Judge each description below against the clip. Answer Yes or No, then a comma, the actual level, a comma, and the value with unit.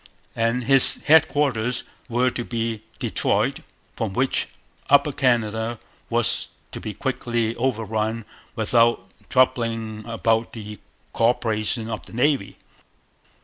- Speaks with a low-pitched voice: Yes, low, 115 Hz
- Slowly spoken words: Yes, slow, 110 wpm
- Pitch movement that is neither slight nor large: No, narrow, 2.2 semitones